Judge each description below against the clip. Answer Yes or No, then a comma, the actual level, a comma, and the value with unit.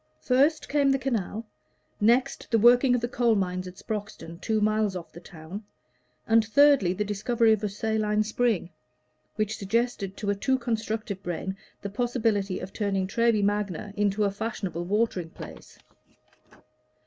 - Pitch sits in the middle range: No, high, 215 Hz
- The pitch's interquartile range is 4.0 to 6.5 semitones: No, average, 2.9 semitones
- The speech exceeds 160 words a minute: No, average, 155 wpm